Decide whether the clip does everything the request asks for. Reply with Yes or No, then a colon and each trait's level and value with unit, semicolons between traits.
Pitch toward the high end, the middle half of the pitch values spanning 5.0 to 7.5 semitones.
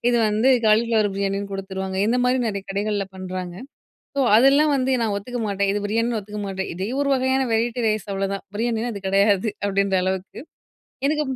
No: high, 210 Hz; average, 3.3 semitones